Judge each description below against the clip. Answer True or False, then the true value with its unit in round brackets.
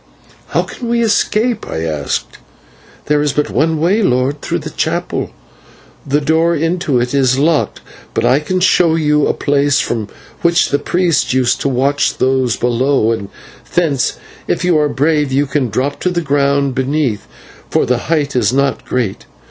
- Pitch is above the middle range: False (140 Hz)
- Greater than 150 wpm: True (170 wpm)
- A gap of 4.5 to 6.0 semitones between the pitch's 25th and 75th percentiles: False (4.1 semitones)